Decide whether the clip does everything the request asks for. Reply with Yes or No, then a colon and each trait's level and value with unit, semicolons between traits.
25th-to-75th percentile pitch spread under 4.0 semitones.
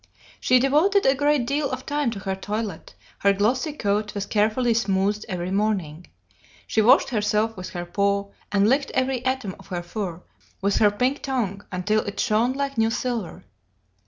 No: average, 4.5 semitones